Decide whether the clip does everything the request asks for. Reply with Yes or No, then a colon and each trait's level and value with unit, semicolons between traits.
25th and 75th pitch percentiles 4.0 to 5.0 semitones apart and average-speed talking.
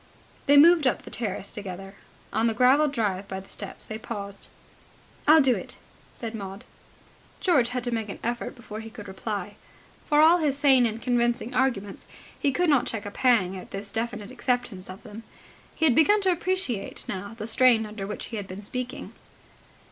Yes: average, 4.3 semitones; average, 190 wpm